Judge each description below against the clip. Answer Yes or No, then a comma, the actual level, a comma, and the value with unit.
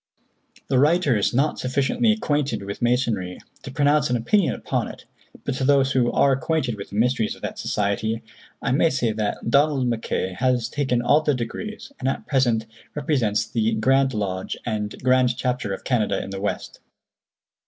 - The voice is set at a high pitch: No, low, 125 Hz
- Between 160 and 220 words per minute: Yes, average, 175 wpm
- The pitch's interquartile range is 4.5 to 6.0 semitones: No, average, 4.1 semitones